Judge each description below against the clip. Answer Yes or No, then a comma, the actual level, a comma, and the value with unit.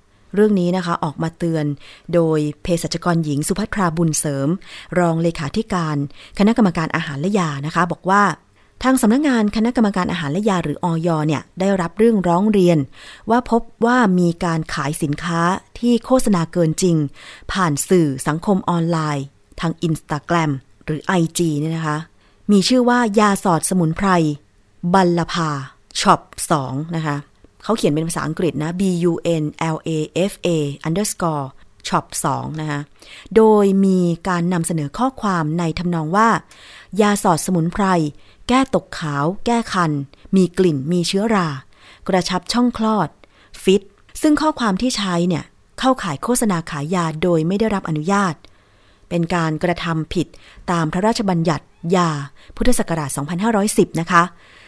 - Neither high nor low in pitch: Yes, medium, 170 Hz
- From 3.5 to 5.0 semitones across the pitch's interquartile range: Yes, average, 4.2 semitones